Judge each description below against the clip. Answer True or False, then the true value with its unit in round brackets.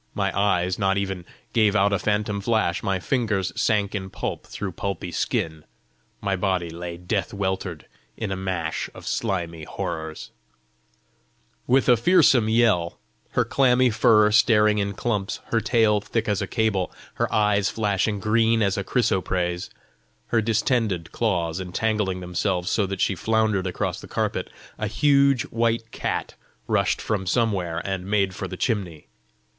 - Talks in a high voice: False (100 Hz)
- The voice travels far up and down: False (3.3 semitones)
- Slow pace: False (155 wpm)